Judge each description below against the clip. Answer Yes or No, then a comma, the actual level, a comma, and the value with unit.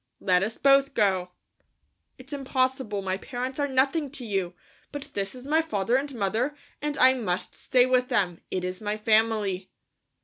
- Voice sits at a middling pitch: No, high, 245 Hz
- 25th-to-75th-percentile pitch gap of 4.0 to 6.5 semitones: Yes, wide, 5.5 semitones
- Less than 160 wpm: No, average, 170 wpm